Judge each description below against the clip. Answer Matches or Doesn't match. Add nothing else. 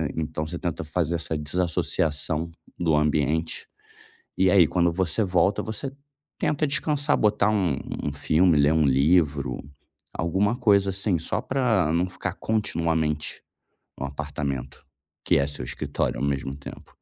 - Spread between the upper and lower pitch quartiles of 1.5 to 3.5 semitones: Doesn't match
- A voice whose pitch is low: Matches